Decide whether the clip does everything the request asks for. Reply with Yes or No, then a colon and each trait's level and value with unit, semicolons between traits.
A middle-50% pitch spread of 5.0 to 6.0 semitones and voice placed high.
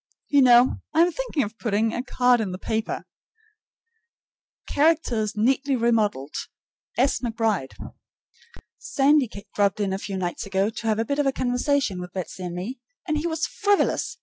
Yes: wide, 5.4 semitones; high, 235 Hz